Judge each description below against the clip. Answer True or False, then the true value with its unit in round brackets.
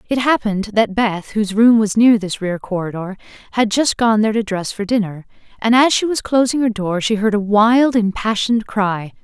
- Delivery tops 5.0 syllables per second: True (5.2 syllables/s)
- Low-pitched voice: False (215 Hz)